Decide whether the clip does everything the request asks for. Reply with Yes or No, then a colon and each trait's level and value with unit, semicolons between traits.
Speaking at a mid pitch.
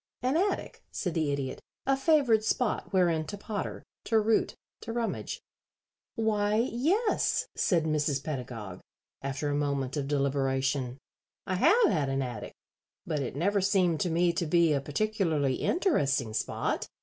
Yes: medium, 165 Hz